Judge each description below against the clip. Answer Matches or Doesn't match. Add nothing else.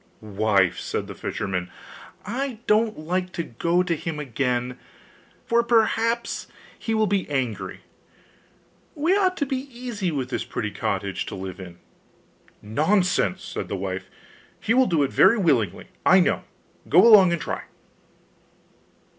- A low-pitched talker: Doesn't match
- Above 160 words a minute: Doesn't match